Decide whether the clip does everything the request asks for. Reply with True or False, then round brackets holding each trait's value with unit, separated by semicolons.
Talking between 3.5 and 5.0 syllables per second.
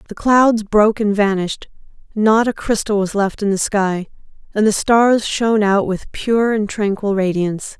True (4.6 syllables/s)